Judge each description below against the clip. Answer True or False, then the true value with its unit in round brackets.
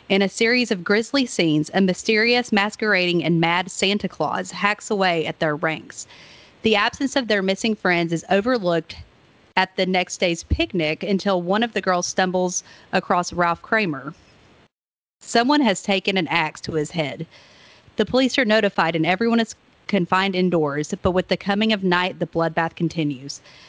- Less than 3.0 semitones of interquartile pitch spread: False (3.8 semitones)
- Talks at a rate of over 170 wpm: False (165 wpm)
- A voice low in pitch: False (185 Hz)